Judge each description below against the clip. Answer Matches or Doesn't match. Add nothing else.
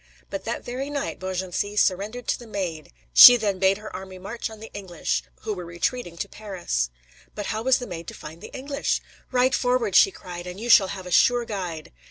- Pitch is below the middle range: Doesn't match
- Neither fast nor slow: Doesn't match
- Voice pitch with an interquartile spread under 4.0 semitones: Doesn't match